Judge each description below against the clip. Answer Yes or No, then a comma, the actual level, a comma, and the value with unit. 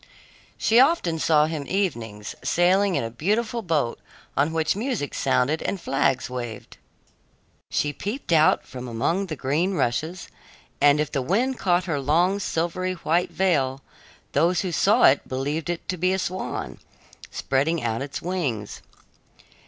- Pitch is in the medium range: Yes, medium, 160 Hz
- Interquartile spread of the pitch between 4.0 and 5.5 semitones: Yes, average, 5.2 semitones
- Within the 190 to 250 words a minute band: No, average, 150 wpm